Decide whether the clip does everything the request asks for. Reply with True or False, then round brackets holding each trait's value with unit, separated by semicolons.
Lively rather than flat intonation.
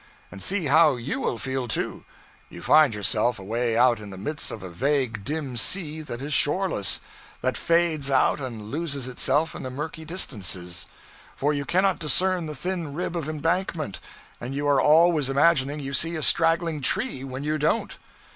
False (4.6 semitones)